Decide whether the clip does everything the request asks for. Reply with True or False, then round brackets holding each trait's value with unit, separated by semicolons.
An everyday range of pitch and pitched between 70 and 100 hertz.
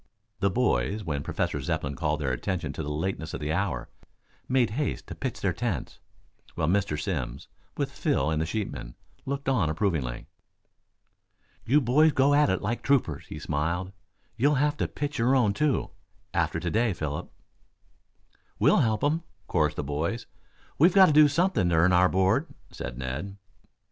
False (8.7 semitones; 95 Hz)